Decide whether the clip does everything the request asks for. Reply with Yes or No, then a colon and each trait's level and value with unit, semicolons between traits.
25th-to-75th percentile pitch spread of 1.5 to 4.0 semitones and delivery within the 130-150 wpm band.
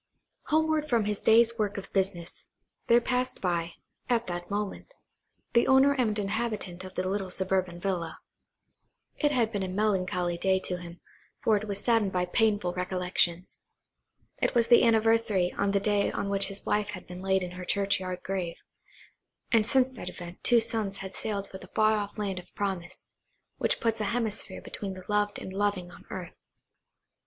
No: average, 3.3 semitones; average, 180 wpm